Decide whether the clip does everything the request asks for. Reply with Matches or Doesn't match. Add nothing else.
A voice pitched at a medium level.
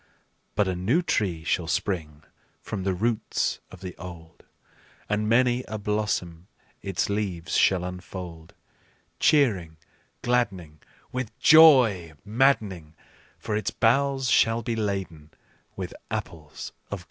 Doesn't match